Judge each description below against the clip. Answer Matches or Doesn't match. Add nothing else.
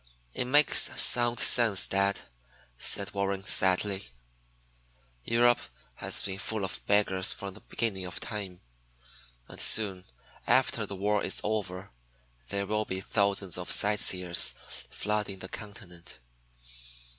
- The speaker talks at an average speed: Doesn't match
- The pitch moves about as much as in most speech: Doesn't match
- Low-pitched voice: Matches